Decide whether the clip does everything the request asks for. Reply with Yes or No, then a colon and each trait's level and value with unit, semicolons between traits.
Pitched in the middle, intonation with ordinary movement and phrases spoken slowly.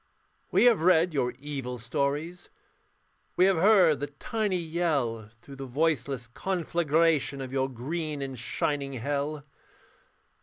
Yes: medium, 145 Hz; average, 3.9 semitones; slow, 125 wpm